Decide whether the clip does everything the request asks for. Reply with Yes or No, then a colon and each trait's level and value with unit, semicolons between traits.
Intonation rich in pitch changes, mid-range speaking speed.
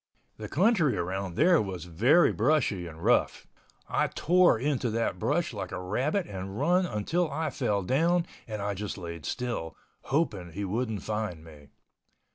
Yes: wide, 8.4 semitones; average, 160 wpm